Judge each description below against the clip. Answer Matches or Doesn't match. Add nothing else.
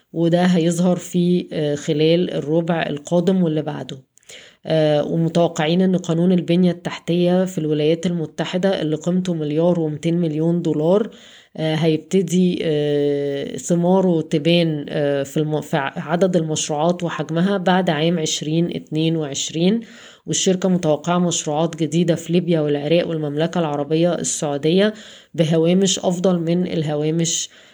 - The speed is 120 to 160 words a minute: Doesn't match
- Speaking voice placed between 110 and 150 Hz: Doesn't match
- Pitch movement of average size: Doesn't match